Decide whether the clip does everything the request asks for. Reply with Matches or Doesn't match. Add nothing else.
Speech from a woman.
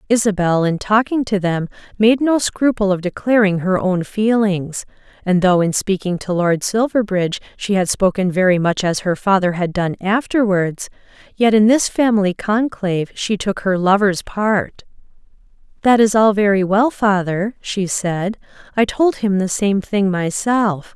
Matches